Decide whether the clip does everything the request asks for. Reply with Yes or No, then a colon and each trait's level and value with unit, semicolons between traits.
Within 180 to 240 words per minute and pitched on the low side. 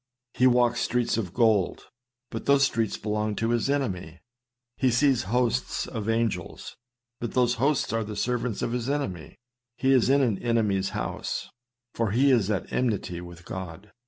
No: average, 165 wpm; low, 115 Hz